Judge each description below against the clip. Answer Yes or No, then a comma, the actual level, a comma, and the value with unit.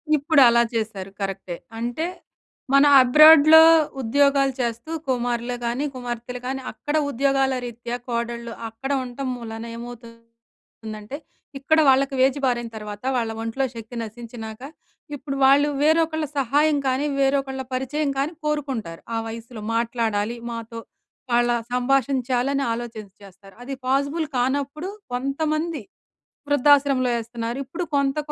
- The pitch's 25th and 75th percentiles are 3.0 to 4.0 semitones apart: Yes, average, 3.3 semitones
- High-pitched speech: Yes, very high, 250 Hz